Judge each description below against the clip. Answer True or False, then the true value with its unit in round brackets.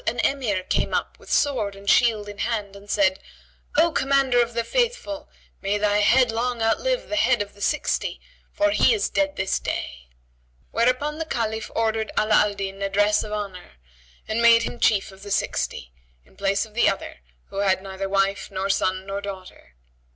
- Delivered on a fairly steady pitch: False (3.6 semitones)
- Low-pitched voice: False (210 Hz)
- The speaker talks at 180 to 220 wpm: True (190 wpm)